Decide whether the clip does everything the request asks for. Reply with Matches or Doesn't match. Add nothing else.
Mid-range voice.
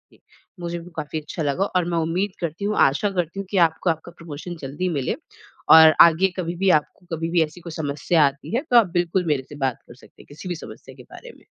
Matches